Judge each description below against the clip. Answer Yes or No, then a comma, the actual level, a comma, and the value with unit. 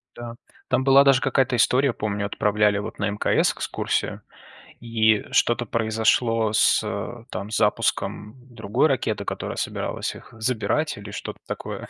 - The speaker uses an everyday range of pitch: Yes, average, 3.1 semitones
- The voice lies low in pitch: Yes, low, 115 Hz